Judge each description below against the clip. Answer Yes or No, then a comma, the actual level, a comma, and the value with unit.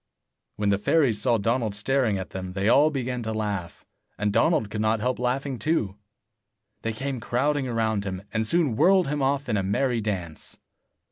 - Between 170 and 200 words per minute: Yes, average, 185 wpm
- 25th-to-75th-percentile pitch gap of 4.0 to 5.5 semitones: Yes, average, 4.5 semitones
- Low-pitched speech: Yes, low, 115 Hz